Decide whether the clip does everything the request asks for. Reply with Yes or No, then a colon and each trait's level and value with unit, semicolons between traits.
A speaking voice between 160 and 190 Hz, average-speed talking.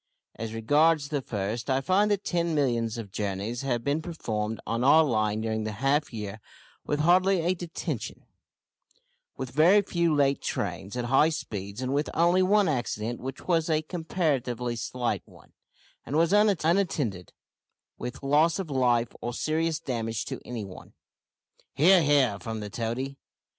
No: low, 135 Hz; average, 165 wpm